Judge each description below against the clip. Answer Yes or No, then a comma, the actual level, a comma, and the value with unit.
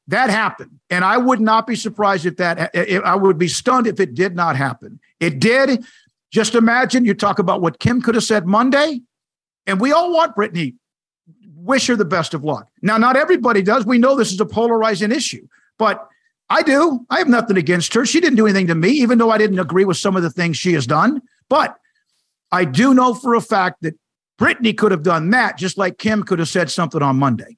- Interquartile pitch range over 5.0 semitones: Yes, wide, 5.4 semitones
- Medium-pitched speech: No, high, 210 Hz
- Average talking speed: No, fast, 225 wpm